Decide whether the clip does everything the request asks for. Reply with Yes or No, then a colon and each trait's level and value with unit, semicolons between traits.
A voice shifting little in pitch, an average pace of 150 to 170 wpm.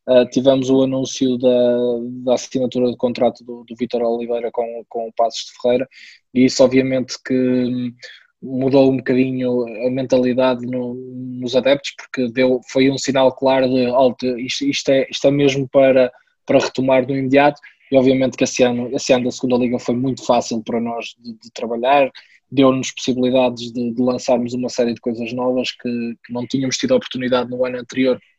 No: narrow, 1.3 semitones; fast, 185 wpm